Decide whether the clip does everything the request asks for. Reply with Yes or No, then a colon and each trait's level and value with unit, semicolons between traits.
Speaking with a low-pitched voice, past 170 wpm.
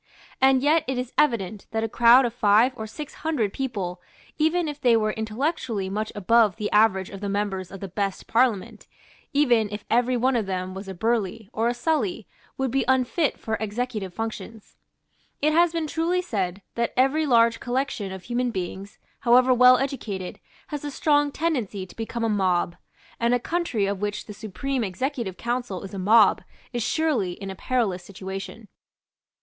No: high, 230 Hz; average, 180 wpm